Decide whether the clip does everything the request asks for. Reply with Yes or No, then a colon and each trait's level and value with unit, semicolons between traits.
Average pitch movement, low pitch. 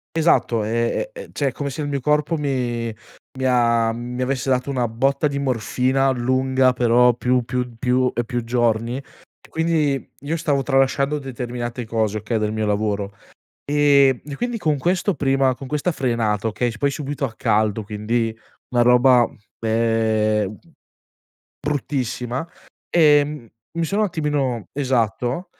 Yes: average, 3.3 semitones; low, 125 Hz